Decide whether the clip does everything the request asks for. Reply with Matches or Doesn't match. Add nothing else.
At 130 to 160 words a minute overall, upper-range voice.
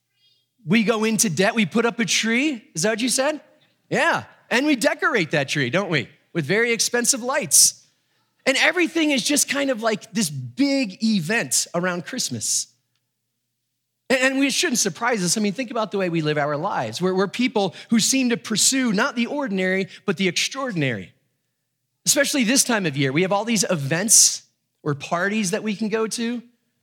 Doesn't match